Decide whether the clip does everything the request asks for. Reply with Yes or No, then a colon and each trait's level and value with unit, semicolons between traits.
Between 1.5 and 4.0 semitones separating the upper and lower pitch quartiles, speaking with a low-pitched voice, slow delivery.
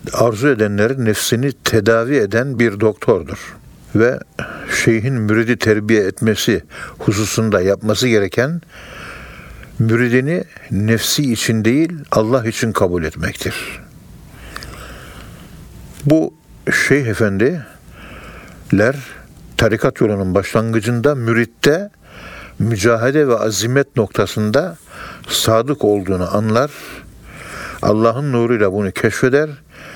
Yes: average, 3.4 semitones; low, 115 Hz; slow, 80 wpm